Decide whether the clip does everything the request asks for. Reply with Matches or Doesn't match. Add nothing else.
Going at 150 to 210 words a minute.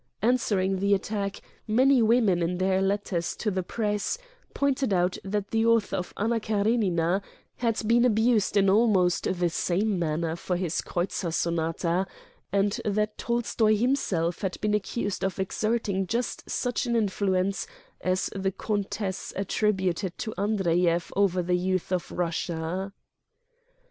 Doesn't match